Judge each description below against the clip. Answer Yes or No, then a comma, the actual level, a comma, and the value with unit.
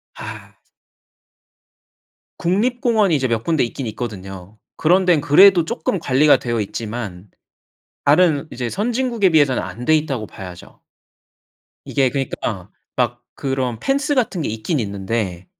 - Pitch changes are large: Yes, wide, 8.0 semitones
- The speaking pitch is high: No, low, 135 Hz